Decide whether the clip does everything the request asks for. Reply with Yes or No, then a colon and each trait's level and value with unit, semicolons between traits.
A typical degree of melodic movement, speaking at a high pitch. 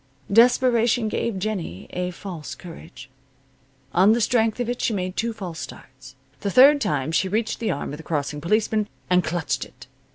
No: wide, 5.8 semitones; high, 195 Hz